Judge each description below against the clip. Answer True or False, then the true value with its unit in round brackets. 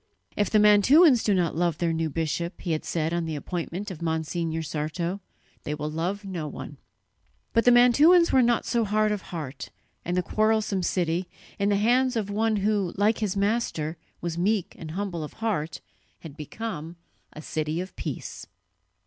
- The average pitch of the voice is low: False (180 Hz)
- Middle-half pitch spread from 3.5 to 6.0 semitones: True (4.8 semitones)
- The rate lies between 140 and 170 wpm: False (180 wpm)